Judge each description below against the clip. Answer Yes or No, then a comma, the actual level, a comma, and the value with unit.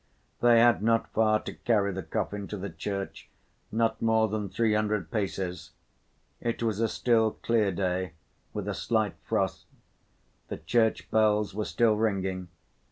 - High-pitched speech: No, low, 105 Hz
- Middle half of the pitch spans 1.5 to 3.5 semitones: Yes, narrow, 2.4 semitones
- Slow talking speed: No, average, 155 wpm